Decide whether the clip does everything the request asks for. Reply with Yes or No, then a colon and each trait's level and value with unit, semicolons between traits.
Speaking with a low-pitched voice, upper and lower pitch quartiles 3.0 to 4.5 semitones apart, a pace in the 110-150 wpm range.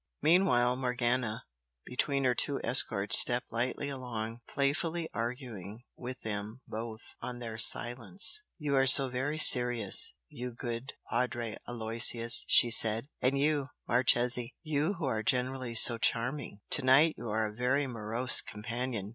No: low, 125 Hz; narrow, 2.6 semitones; average, 140 wpm